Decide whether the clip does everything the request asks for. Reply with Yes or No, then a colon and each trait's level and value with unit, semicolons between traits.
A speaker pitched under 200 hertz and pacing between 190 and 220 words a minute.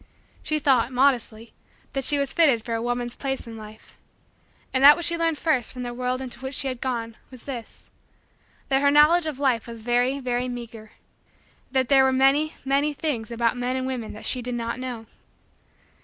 No: very high, 255 Hz; average, 200 wpm